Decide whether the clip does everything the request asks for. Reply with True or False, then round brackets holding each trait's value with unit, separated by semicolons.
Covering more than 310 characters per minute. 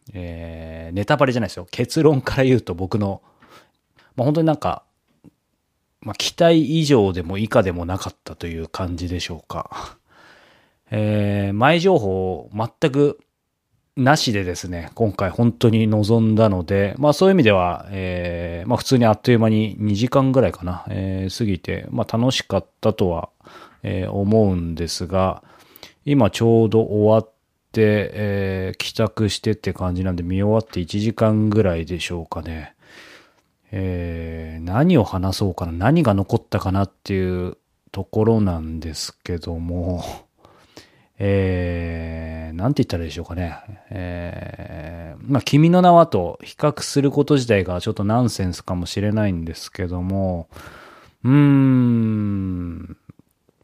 False (290 characters per minute)